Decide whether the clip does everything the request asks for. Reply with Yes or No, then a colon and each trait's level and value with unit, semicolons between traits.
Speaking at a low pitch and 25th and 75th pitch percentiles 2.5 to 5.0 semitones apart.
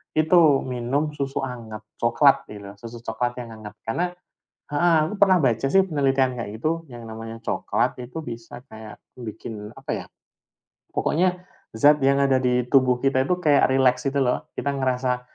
Yes: low, 130 Hz; average, 3.9 semitones